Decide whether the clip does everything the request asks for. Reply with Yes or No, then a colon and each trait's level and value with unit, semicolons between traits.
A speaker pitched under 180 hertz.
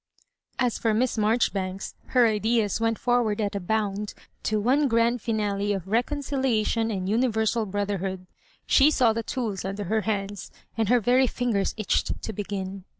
No: high, 220 Hz